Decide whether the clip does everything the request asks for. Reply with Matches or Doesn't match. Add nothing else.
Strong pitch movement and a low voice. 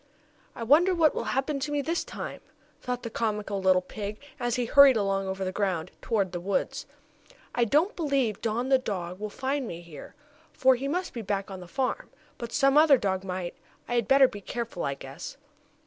Doesn't match